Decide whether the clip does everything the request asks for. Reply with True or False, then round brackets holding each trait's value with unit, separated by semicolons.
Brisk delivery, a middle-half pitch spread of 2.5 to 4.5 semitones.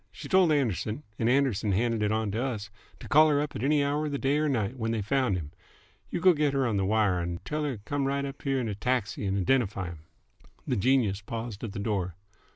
False (245 wpm; 5.4 semitones)